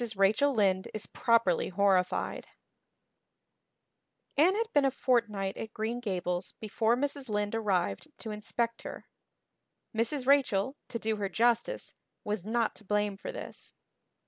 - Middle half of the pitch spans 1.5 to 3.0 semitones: No, average, 3.6 semitones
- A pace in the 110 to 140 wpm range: Yes, slow, 135 wpm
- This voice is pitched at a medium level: No, high, 220 Hz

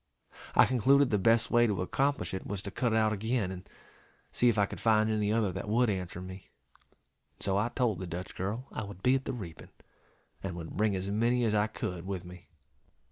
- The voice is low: Yes, low, 105 Hz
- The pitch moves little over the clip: No, average, 3.8 semitones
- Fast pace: Yes, fast, 220 wpm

